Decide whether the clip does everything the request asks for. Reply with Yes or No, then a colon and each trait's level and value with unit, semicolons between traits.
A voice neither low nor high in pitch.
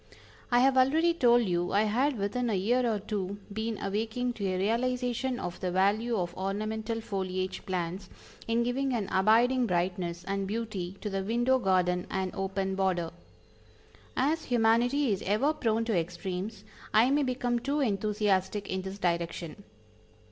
No: high, 210 Hz